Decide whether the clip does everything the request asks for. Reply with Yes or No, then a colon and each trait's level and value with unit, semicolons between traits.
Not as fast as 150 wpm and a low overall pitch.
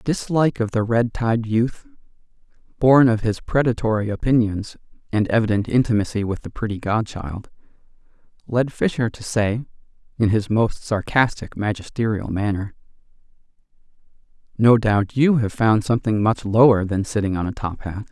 Yes: average, 140 wpm; low, 110 Hz